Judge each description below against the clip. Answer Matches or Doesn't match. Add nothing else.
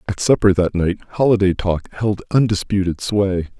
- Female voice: Doesn't match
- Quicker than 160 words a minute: Doesn't match